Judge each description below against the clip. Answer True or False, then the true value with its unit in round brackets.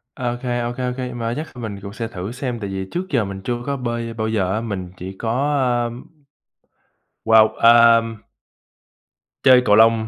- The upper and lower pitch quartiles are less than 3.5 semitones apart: True (2.4 semitones)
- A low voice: True (115 Hz)